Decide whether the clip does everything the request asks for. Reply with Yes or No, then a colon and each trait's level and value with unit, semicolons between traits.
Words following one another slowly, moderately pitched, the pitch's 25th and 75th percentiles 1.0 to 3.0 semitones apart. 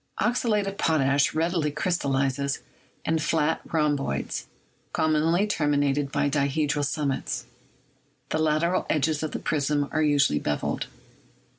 Yes: slow, 120 wpm; medium, 150 Hz; narrow, 2.4 semitones